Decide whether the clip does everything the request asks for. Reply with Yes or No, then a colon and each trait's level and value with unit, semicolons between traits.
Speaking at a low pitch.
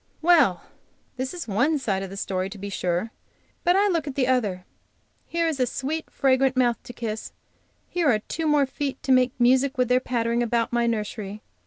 No: very high, 250 Hz